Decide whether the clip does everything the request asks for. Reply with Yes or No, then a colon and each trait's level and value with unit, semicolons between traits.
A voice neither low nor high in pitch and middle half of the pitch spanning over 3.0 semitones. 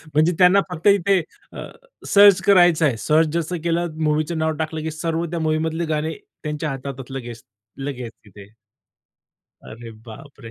Yes: medium, 155 Hz; average, 3.5 semitones